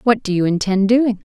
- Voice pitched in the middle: No, high, 210 Hz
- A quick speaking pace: Yes, fast, 220 wpm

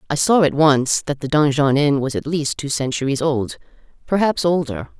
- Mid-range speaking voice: Yes, medium, 145 Hz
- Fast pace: No, average, 180 wpm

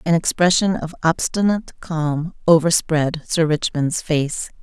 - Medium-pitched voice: Yes, medium, 165 Hz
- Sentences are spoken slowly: Yes, slow, 115 wpm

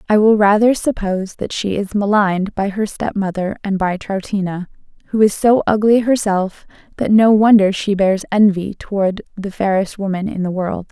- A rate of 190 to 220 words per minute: No, average, 175 wpm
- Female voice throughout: Yes, female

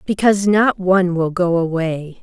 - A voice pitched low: No, medium, 185 Hz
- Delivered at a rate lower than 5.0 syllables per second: Yes, 4.8 syllables/s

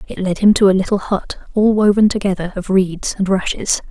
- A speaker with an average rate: No, fast, 215 wpm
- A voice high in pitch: Yes, high, 195 Hz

